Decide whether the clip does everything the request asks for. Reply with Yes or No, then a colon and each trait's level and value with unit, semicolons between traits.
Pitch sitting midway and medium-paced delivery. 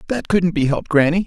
No: medium, 165 Hz; fast, 240 wpm